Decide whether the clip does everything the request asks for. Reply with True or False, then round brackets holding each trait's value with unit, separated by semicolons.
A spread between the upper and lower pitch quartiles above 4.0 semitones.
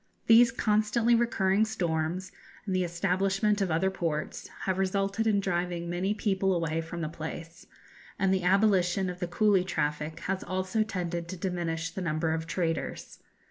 False (2.7 semitones)